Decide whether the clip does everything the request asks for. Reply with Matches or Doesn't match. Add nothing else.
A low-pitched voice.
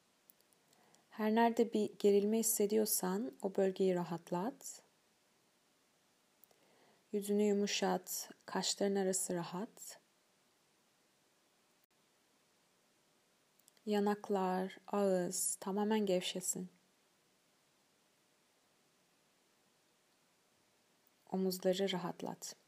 Doesn't match